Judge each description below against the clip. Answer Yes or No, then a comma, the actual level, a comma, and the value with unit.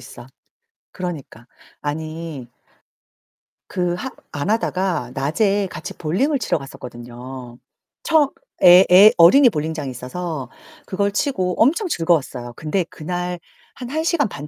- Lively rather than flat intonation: Yes, wide, 6.0 semitones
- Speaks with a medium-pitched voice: Yes, medium, 175 Hz